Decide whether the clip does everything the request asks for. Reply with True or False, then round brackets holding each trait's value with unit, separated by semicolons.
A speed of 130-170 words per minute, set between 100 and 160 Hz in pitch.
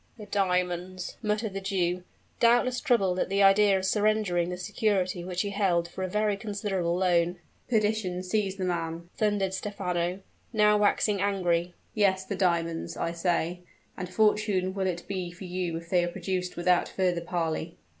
False (165 wpm; 185 Hz)